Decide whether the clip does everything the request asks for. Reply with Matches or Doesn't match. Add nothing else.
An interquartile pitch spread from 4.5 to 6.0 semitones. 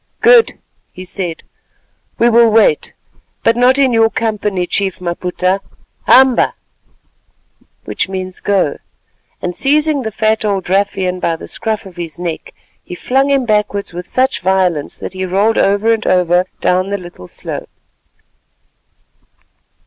Doesn't match